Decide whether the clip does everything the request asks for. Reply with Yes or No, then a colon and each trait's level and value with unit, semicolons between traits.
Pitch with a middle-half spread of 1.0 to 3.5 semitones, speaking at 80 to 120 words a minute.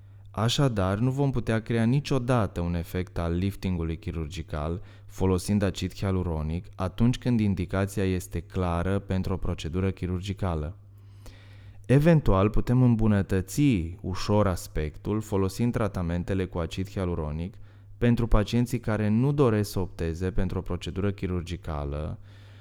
Yes: average, 2.9 semitones; slow, 115 wpm